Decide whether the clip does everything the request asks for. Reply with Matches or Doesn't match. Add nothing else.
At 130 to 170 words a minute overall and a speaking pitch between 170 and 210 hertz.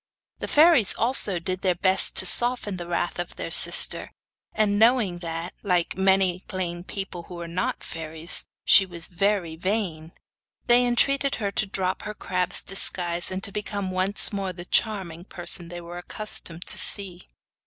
Matches